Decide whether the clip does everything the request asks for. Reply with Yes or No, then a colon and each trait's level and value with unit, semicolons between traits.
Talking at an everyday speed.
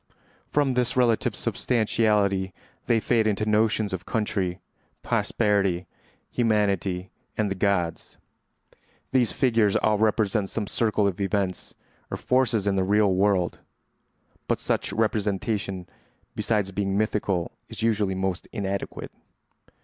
No: slow, 120 wpm